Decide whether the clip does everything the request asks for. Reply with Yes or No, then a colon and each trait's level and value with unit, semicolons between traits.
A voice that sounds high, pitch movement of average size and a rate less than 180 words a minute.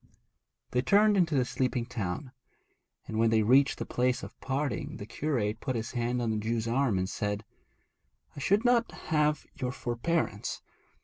No: low, 125 Hz; average, 4.5 semitones; average, 170 wpm